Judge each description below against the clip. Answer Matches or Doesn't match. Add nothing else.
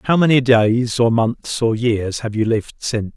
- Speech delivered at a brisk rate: Matches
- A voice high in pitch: Doesn't match